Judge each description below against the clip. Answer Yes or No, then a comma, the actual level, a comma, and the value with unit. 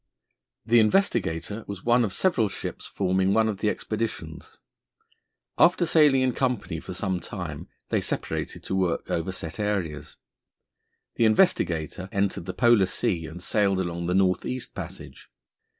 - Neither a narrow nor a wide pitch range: Yes, average, 4.3 semitones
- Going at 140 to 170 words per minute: Yes, average, 150 wpm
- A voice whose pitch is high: No, low, 100 Hz